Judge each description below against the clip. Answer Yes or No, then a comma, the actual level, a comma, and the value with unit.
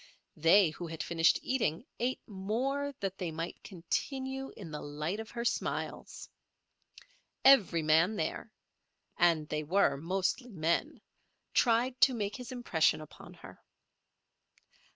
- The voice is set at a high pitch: Yes, high, 195 Hz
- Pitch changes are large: Yes, wide, 7.0 semitones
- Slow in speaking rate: Yes, slow, 120 wpm